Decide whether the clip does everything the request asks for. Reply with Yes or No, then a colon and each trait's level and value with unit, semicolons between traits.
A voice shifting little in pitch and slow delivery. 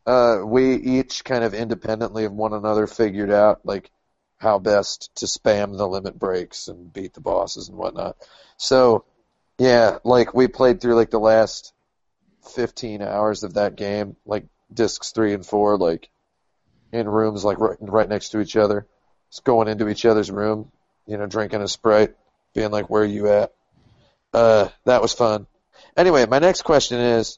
No: narrow, 2.0 semitones; average, 175 wpm